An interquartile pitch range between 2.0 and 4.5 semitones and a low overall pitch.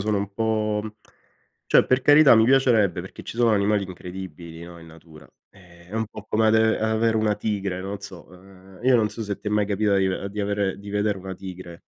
Yes: average, 2.7 semitones; low, 100 Hz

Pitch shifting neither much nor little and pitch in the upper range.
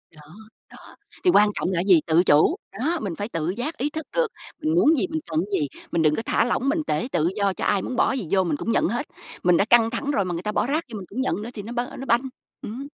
No: wide, 7.4 semitones; high, 220 Hz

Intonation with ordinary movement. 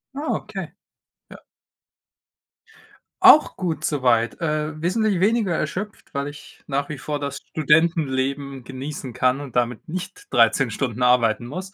Yes: average, 5.0 semitones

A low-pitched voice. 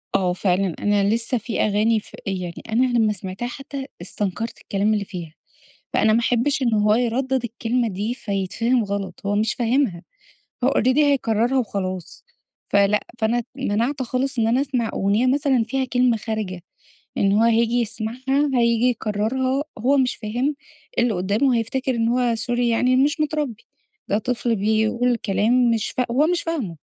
No: high, 230 Hz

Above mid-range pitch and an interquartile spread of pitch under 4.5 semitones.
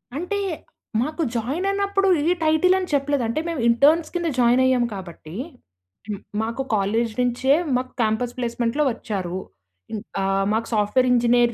No: high, 245 Hz; average, 5.3 semitones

